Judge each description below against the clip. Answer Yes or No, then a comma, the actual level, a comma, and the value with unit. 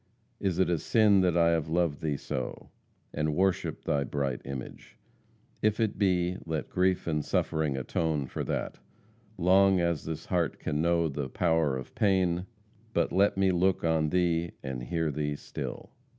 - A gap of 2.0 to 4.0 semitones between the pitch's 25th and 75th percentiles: Yes, average, 3.5 semitones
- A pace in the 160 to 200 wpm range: Yes, average, 165 wpm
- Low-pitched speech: Yes, very low, 85 Hz